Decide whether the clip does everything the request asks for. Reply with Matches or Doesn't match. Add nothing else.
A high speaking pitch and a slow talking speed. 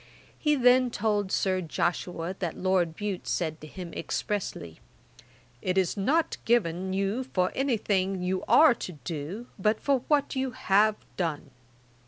Doesn't match